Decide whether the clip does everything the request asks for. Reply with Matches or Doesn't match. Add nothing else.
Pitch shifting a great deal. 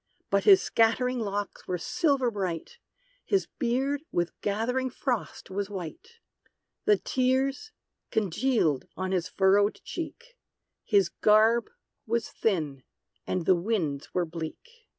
Matches